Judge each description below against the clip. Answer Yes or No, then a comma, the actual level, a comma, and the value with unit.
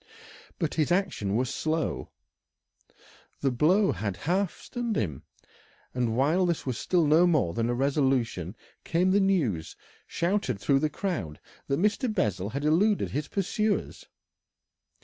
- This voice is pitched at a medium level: Yes, medium, 150 Hz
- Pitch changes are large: Yes, wide, 7.6 semitones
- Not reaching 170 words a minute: Yes, average, 140 wpm